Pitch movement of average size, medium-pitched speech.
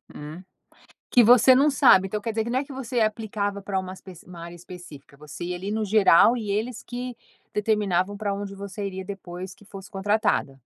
No: average, 3.2 semitones; high, 200 Hz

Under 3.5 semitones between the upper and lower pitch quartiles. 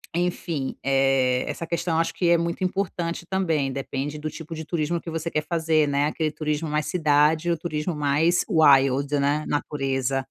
Yes: average, 2.9 semitones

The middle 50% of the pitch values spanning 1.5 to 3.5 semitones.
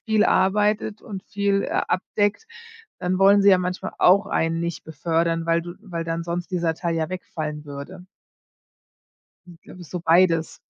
Yes: average, 2.8 semitones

